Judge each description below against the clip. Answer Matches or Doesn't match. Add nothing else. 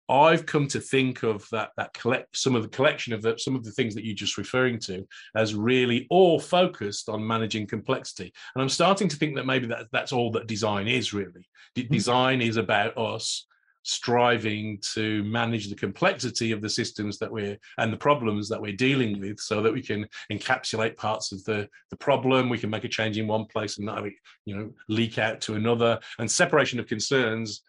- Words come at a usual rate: Doesn't match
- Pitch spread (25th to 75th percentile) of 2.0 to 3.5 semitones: Matches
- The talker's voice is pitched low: Matches